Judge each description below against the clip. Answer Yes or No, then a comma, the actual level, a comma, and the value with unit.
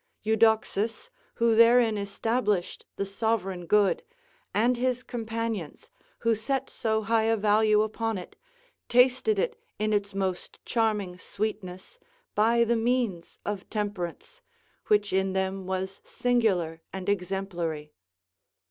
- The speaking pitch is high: Yes, high, 215 Hz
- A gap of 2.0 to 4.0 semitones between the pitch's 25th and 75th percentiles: Yes, average, 3.2 semitones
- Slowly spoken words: Yes, slow, 120 wpm